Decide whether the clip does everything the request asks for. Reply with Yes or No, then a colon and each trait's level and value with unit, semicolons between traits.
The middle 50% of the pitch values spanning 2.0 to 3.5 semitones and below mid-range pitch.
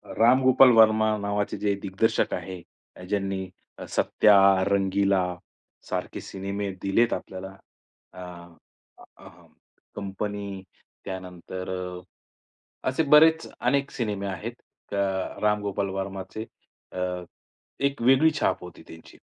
Yes: average, 2.7 semitones; low, 100 Hz